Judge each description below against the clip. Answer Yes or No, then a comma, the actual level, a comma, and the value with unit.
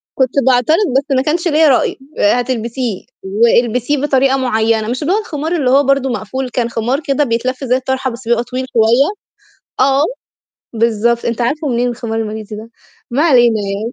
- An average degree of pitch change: Yes, average, 3.0 semitones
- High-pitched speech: Yes, very high, 250 Hz